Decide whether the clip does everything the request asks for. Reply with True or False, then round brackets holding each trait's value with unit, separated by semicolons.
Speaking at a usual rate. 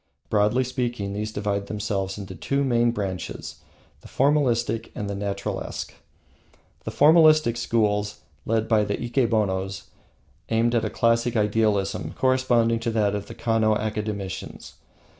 False (130 wpm)